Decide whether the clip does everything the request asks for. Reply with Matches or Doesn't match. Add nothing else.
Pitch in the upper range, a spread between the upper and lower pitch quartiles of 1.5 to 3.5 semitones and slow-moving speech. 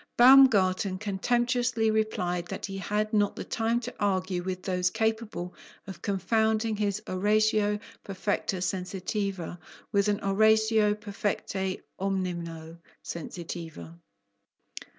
Matches